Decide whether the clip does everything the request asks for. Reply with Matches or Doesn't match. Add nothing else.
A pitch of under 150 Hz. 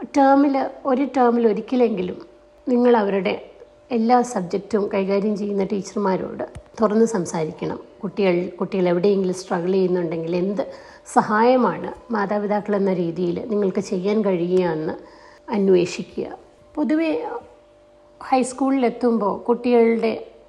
Doesn't match